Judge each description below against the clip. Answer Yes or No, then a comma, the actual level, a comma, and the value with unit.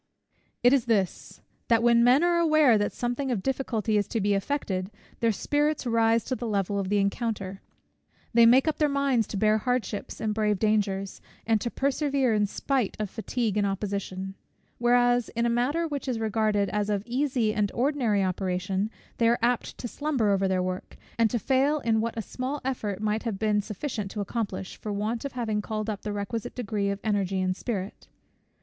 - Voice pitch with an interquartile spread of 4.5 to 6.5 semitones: No, average, 3.5 semitones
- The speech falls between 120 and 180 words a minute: No, average, 195 wpm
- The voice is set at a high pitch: Yes, high, 220 Hz